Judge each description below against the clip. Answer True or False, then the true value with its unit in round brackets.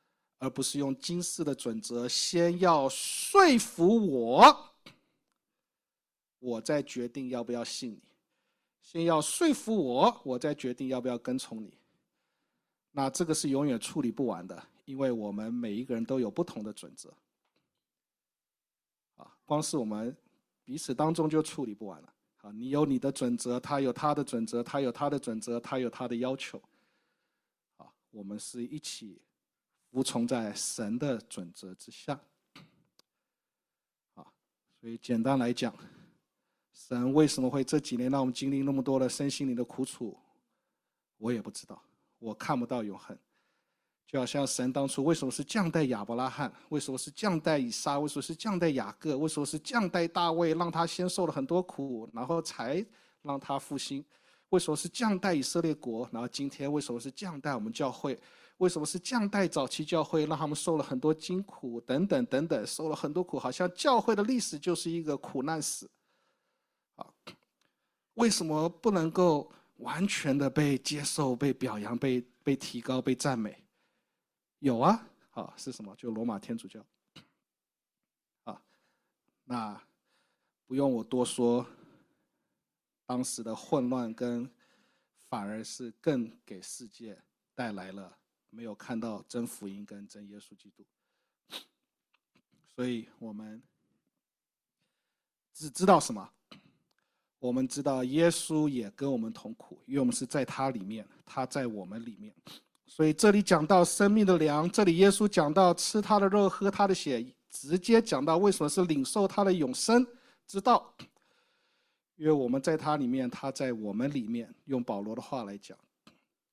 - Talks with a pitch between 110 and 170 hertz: True (140 Hz)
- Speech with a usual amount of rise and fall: False (5.9 semitones)